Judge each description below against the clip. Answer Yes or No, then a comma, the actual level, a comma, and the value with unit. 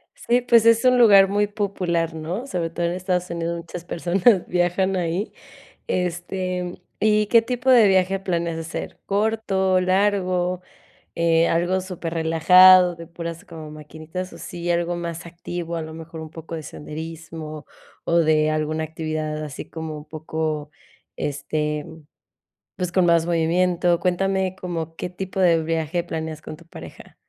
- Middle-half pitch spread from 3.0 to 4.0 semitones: No, narrow, 2.5 semitones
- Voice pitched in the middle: Yes, medium, 170 Hz